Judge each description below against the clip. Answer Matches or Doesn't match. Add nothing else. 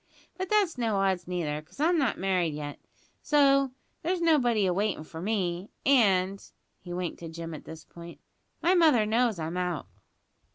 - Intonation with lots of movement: Matches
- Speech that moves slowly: Doesn't match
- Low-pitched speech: Doesn't match